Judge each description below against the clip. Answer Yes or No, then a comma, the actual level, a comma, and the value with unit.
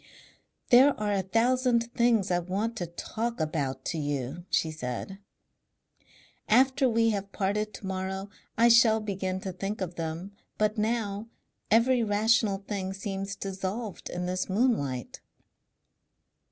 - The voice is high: Yes, high, 200 Hz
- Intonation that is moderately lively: Yes, average, 3.7 semitones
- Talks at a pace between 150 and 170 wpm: No, slow, 135 wpm